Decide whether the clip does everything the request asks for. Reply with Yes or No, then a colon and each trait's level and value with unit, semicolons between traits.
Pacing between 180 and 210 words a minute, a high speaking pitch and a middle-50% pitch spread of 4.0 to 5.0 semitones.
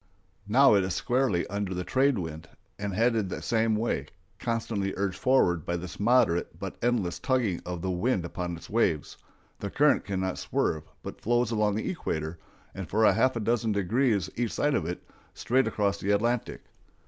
No: average, 185 wpm; low, 105 Hz; average, 4.7 semitones